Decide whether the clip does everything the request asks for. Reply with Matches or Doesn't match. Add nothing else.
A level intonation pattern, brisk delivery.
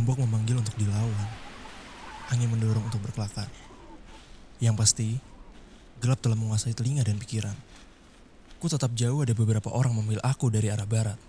Matches